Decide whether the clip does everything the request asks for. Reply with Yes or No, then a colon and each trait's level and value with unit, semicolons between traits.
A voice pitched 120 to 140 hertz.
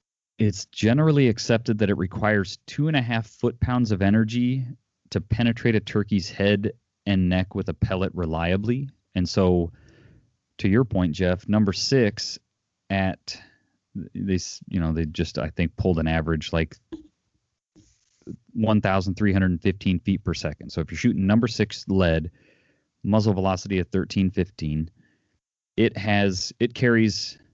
No: low, 100 Hz